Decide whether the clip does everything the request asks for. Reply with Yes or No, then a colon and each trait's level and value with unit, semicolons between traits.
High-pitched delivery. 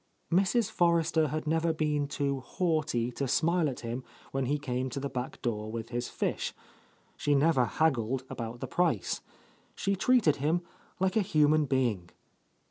No: medium, 145 Hz